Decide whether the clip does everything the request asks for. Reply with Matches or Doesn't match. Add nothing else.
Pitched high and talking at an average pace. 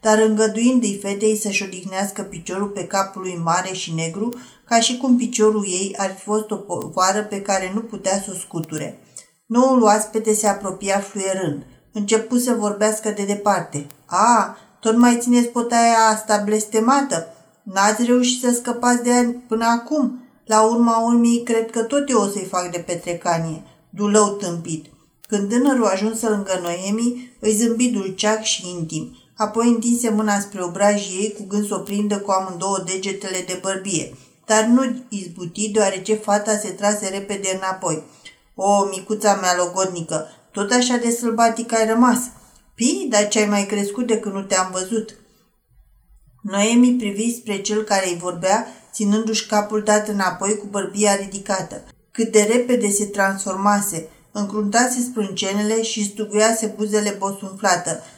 Matches